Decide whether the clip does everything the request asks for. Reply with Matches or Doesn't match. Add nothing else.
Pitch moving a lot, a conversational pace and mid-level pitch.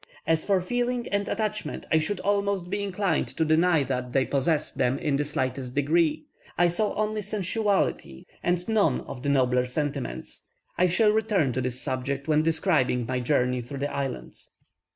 Matches